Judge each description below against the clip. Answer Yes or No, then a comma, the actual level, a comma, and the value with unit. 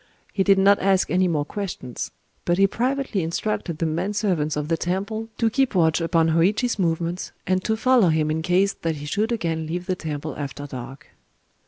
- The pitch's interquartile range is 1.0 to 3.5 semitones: No, average, 4.0 semitones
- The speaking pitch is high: No, medium, 175 Hz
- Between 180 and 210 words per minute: Yes, average, 195 wpm